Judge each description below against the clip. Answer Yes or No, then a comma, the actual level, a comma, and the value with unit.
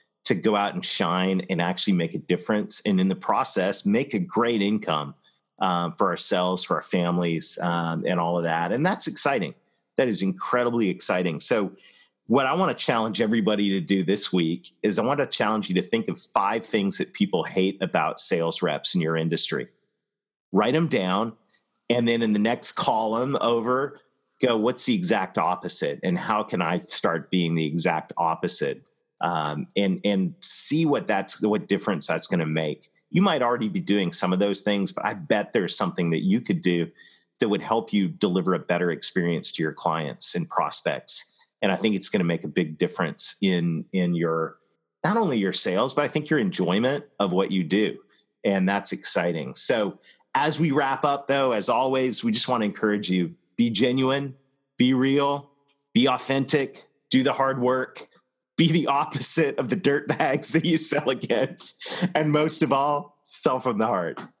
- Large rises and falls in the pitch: Yes, wide, 7.5 semitones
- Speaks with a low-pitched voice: Yes, low, 105 Hz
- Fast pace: No, average, 190 wpm